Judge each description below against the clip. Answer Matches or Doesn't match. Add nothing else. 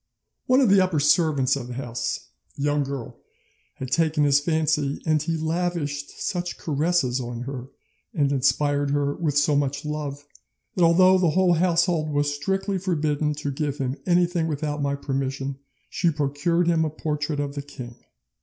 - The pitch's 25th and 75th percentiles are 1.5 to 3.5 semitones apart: Matches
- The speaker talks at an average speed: Matches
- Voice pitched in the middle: Matches